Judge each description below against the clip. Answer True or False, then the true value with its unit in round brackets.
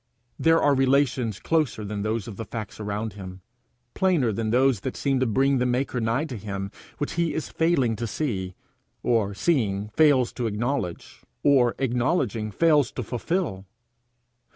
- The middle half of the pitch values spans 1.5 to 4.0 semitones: False (4.7 semitones)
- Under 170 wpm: True (160 wpm)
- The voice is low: True (120 Hz)